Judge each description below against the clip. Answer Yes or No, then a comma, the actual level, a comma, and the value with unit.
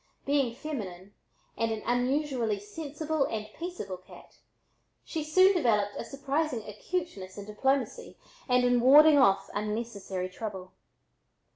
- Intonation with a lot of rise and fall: Yes, wide, 6.1 semitones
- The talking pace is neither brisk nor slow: No, slow, 120 wpm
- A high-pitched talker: Yes, high, 245 Hz